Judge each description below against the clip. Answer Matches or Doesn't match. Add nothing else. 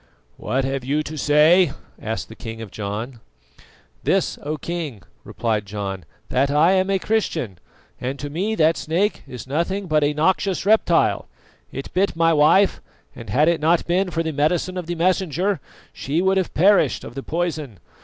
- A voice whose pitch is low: Doesn't match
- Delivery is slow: Doesn't match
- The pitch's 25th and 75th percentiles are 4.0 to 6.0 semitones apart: Matches